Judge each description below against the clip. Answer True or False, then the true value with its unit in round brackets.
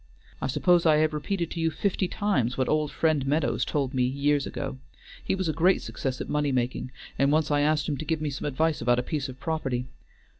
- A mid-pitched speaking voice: True (150 Hz)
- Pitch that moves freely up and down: False (3.1 semitones)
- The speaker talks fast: True (230 wpm)